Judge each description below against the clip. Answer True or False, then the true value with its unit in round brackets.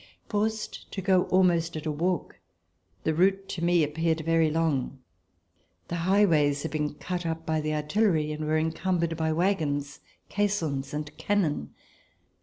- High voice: False (165 Hz)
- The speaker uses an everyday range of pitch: True (3.2 semitones)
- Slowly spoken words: False (155 wpm)